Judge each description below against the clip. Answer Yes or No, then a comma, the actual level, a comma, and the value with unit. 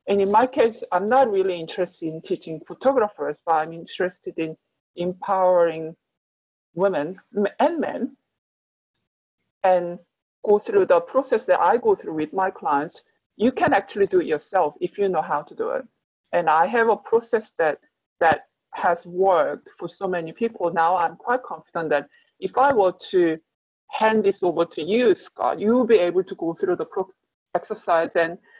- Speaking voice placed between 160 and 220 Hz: Yes, high, 190 Hz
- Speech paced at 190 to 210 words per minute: No, average, 170 wpm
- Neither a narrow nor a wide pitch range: No, wide, 7.5 semitones